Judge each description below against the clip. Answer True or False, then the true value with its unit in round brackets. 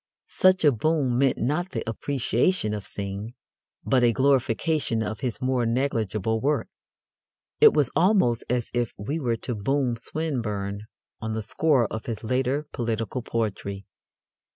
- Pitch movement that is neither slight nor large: True (4.1 semitones)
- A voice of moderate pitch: False (120 Hz)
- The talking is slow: False (145 wpm)